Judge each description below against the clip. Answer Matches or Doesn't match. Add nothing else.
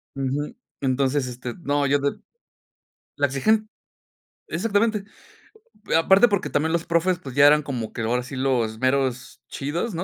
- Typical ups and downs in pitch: Matches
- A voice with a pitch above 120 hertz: Matches